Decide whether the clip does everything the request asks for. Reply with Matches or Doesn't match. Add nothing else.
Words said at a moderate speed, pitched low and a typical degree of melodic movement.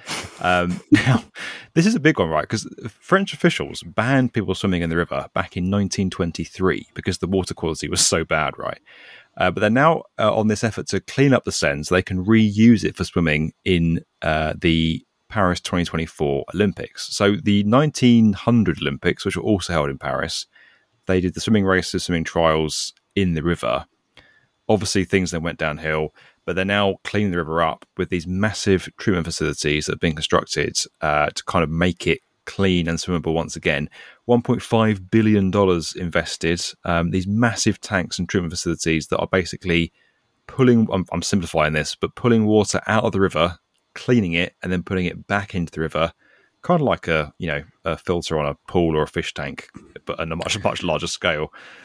Matches